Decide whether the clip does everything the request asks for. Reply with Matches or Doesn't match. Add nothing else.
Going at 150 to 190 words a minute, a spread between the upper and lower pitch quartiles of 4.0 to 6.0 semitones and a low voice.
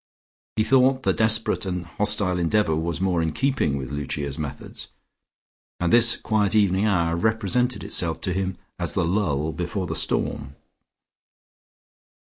Doesn't match